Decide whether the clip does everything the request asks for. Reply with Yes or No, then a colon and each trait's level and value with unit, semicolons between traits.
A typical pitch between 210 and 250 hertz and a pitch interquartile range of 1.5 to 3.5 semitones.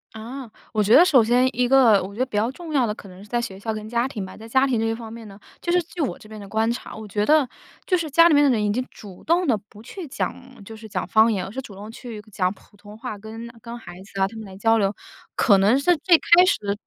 No: high, 225 Hz; average, 4.0 semitones